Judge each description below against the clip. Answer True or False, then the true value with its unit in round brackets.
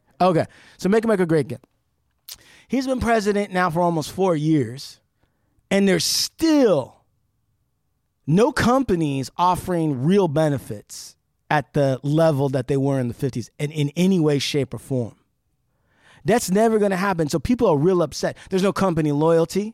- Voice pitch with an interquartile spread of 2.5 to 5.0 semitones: False (5.6 semitones)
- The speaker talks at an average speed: True (165 wpm)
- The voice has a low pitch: False (160 Hz)